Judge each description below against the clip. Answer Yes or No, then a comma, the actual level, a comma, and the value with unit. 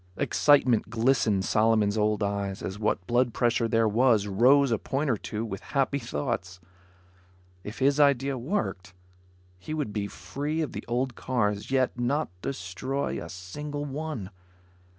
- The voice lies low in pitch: Yes, low, 120 Hz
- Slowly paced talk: No, average, 150 wpm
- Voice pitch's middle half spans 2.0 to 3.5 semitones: No, average, 4.9 semitones